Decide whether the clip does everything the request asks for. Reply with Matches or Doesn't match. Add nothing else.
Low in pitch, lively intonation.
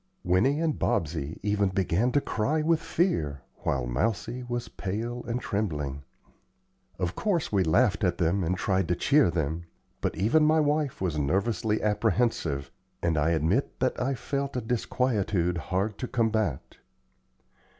Matches